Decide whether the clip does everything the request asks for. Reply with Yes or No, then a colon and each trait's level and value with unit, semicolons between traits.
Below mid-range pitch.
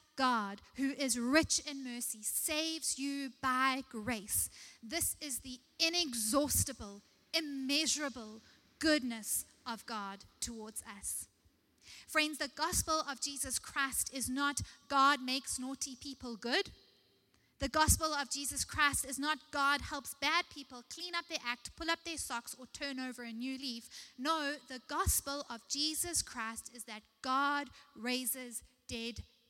No: very high, 275 Hz